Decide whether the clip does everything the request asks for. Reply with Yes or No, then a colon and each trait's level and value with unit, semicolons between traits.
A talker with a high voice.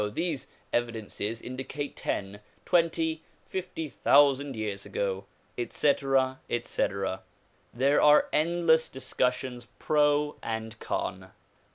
No: low, 135 Hz